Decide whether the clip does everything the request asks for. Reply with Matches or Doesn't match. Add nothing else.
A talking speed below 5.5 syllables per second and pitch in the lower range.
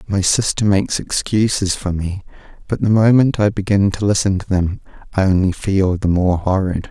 Matches